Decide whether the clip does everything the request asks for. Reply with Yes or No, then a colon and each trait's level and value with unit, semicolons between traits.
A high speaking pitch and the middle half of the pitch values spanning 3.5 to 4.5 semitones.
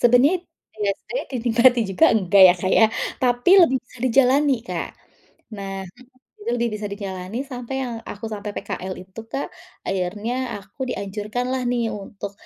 Yes: high, 230 Hz; average, 4.0 semitones